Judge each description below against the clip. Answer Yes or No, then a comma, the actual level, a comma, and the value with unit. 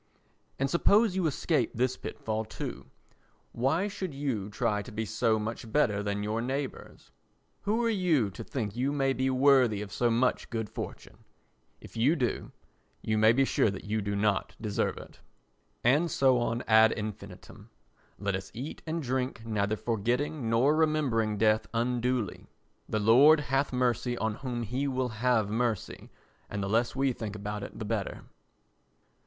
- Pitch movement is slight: No, average, 3.9 semitones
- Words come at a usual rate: Yes, average, 170 wpm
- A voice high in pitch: No, low, 120 Hz